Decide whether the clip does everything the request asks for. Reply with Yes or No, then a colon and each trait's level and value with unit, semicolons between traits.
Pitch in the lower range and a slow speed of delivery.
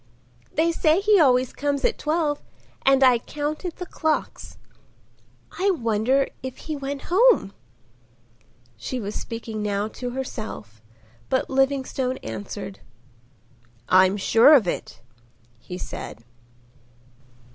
No: very high, 260 Hz; slow, 110 wpm